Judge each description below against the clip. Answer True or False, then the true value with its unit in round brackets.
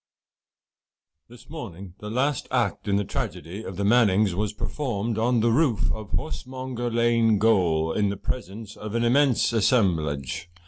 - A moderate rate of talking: True (150 wpm)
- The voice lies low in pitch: True (110 Hz)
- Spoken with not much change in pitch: False (3.6 semitones)